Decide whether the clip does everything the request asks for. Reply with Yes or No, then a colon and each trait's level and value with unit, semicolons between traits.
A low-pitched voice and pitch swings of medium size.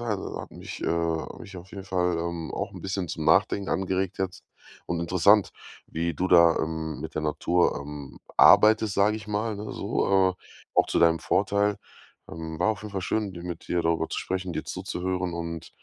Yes: very low, 90 Hz; average, 3.0 semitones